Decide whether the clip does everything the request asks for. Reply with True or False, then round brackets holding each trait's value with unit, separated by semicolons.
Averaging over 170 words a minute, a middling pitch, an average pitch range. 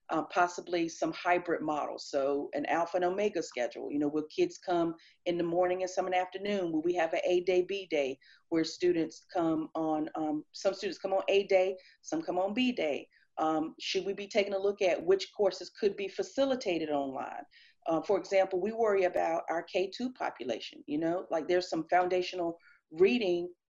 True (200 wpm; 180 Hz; 3.2 semitones)